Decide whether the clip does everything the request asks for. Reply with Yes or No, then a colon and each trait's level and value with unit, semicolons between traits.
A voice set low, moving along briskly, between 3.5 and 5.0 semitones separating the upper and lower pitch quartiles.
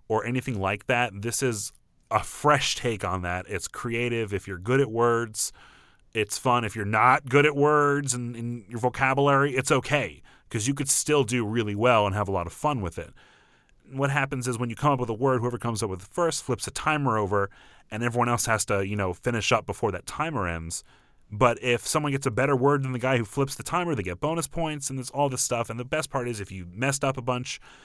Yes: low, 125 Hz; fast, 245 wpm; average, 3.9 semitones